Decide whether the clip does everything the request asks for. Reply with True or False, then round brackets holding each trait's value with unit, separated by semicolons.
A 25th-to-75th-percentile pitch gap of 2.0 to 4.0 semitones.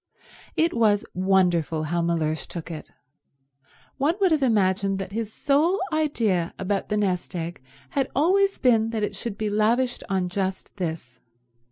False (5.5 semitones)